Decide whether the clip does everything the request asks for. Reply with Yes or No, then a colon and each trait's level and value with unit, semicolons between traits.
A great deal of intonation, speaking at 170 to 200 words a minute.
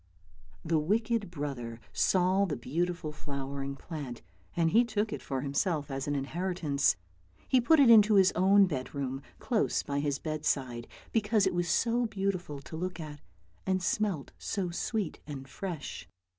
No: wide, 5.9 semitones; average, 155 wpm